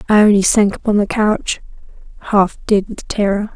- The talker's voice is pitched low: No, high, 205 Hz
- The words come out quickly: No, average, 150 wpm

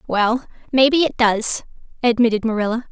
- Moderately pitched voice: No, high, 235 Hz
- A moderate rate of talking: No, slow, 125 wpm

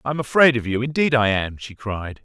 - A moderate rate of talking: No, fast, 240 wpm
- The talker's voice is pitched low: Yes, low, 120 Hz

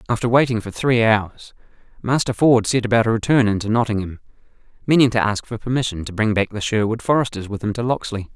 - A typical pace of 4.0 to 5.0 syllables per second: No, 6.1 syllables/s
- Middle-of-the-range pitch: No, low, 115 Hz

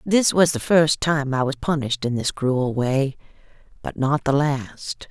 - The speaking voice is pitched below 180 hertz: Yes, medium, 140 Hz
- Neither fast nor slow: Yes, average, 190 wpm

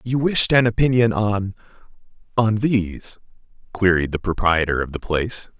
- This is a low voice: Yes, low, 105 Hz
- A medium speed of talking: No, slow, 130 wpm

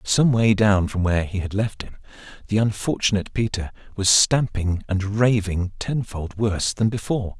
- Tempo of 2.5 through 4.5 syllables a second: No, 5.0 syllables/s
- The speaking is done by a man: Yes, male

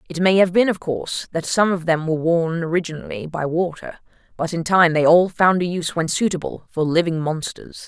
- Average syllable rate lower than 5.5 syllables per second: No, 5.6 syllables/s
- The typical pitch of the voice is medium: Yes, medium, 170 Hz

